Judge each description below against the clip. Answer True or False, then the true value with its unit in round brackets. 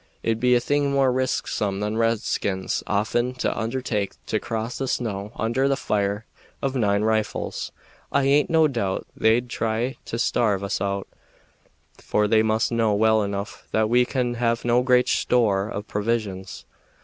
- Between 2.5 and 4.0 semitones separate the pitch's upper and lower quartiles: True (3.1 semitones)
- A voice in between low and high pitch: False (115 Hz)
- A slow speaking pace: False (160 wpm)